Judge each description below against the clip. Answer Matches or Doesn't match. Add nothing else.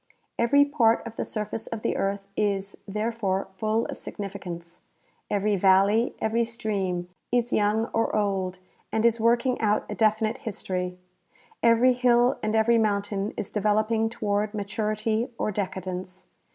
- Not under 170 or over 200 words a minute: Doesn't match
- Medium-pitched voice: Doesn't match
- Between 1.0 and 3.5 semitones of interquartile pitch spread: Matches